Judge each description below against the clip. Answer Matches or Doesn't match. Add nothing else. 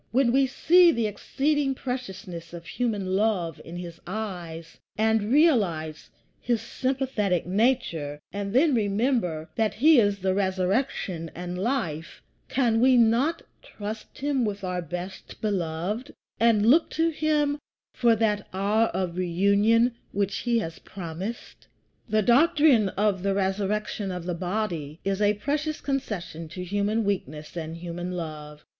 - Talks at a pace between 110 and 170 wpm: Matches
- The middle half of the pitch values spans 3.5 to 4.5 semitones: Doesn't match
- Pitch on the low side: Doesn't match